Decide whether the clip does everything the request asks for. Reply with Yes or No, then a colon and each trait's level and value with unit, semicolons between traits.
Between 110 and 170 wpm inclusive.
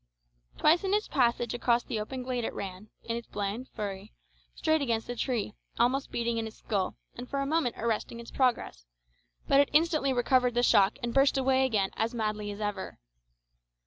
No: average, 190 wpm